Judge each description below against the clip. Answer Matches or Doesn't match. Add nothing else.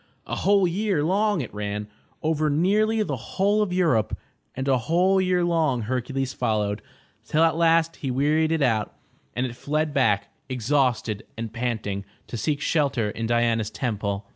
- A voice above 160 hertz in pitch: Doesn't match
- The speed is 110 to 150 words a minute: Doesn't match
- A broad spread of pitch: Matches